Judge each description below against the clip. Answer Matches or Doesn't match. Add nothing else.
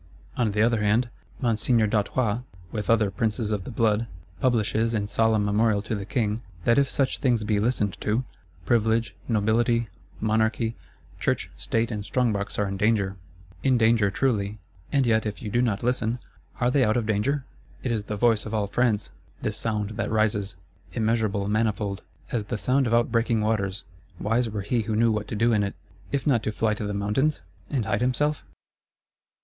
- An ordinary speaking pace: Matches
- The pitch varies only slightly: Matches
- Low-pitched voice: Matches